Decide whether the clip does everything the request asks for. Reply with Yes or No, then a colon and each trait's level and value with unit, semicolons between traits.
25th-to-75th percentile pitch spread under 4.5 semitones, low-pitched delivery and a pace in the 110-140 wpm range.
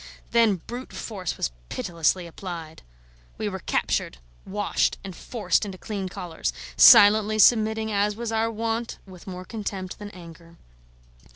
No: average, 3.4 semitones; high, 205 Hz; slow, 135 wpm